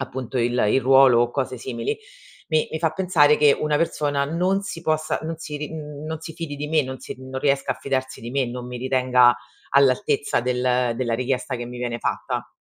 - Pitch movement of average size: Yes, average, 3.3 semitones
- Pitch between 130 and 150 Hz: Yes, low, 135 Hz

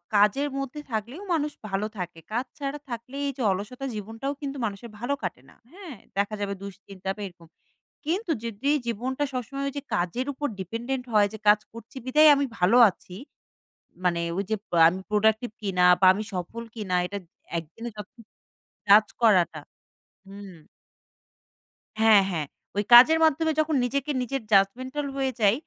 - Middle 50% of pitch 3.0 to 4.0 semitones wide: No, wide, 5.5 semitones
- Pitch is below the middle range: No, high, 225 Hz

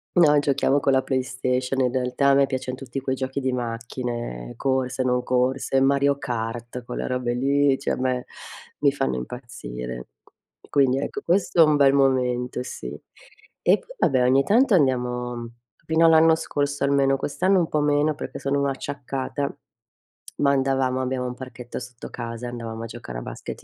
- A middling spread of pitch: No, narrow, 2.2 semitones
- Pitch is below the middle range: Yes, low, 130 Hz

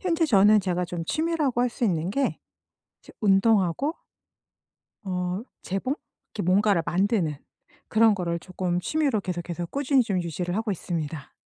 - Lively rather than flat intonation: No, average, 4.8 semitones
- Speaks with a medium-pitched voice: No, high, 195 Hz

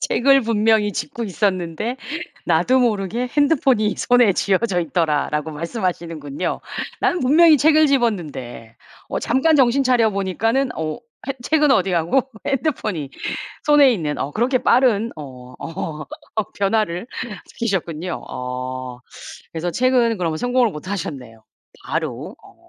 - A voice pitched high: Yes, high, 205 Hz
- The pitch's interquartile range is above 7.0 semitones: Yes, wide, 7.6 semitones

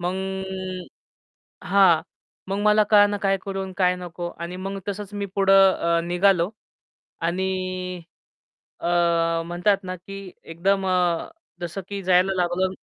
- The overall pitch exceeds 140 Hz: Yes, medium, 185 Hz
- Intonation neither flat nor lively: No, narrow, 1.8 semitones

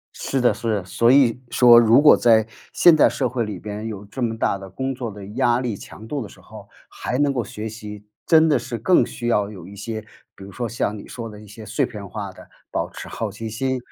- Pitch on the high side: No, low, 115 Hz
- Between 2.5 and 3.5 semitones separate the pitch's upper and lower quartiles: Yes, average, 3.2 semitones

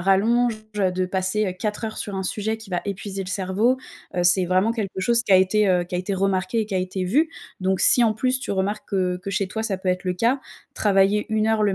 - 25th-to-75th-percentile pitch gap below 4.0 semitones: Yes, average, 2.8 semitones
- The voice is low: No, high, 195 Hz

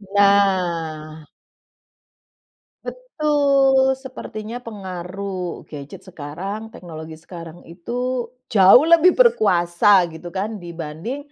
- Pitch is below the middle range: No, high, 190 Hz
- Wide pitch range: Yes, wide, 6.3 semitones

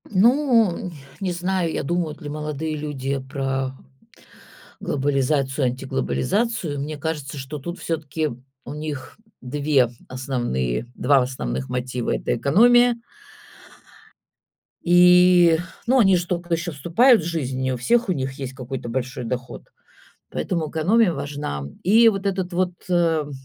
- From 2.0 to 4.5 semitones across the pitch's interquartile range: No, average, 5.2 semitones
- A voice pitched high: No, medium, 150 Hz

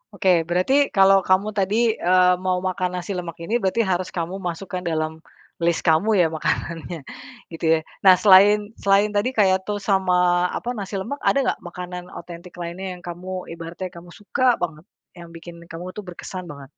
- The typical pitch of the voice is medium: Yes, medium, 180 Hz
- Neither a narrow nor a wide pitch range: No, narrow, 2.1 semitones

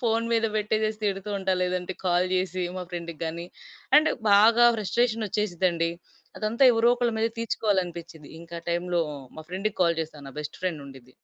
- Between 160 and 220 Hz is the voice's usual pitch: Yes, medium, 185 Hz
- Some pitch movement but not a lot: Yes, average, 4.2 semitones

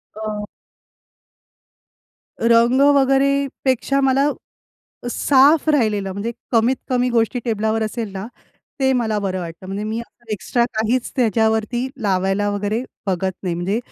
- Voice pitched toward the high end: Yes, high, 220 Hz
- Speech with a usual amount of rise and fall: Yes, average, 3.5 semitones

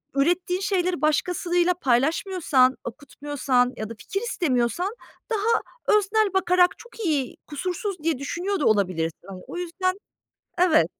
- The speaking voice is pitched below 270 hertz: No, very high, 345 Hz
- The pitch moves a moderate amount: No, wide, 5.8 semitones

